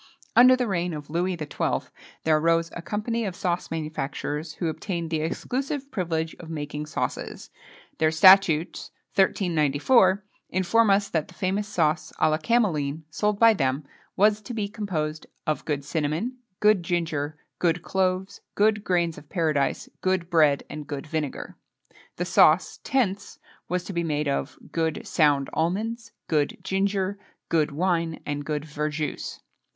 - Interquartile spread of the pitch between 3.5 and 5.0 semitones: Yes, average, 4.4 semitones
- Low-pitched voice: No, medium, 170 Hz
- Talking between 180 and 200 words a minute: No, average, 150 wpm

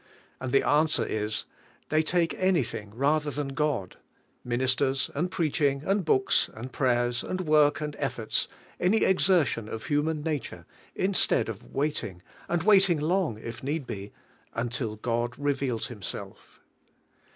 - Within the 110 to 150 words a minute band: Yes, average, 140 wpm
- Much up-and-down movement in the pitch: No, average, 4.8 semitones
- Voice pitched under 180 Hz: Yes, medium, 140 Hz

